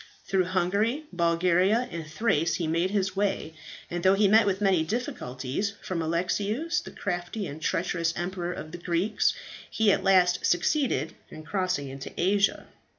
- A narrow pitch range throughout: No, average, 3.1 semitones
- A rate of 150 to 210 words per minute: Yes, average, 155 wpm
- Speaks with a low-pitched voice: No, medium, 180 Hz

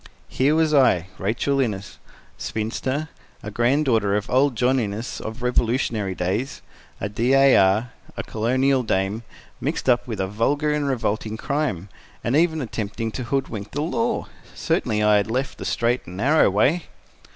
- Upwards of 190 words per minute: No, average, 160 wpm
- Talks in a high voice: No, low, 120 Hz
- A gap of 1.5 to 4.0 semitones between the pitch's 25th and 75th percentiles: No, average, 4.7 semitones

